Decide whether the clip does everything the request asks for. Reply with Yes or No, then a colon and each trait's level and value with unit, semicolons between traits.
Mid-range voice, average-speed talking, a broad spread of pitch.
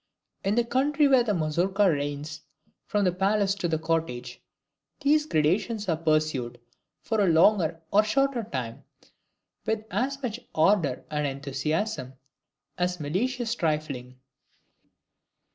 No: medium, 180 Hz; slow, 125 wpm; wide, 6.3 semitones